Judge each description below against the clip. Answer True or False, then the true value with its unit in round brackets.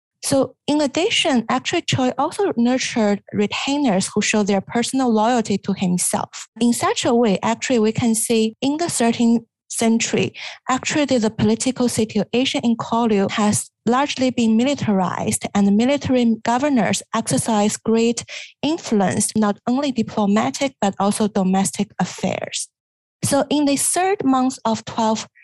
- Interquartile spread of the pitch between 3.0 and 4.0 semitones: True (3.7 semitones)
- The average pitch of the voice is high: True (235 Hz)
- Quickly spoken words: False (140 wpm)